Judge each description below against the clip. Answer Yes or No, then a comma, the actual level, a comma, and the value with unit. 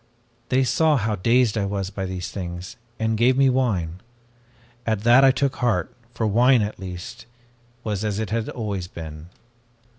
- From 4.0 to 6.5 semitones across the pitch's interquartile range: Yes, average, 4.7 semitones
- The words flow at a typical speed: Yes, average, 170 wpm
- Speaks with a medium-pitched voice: No, low, 110 Hz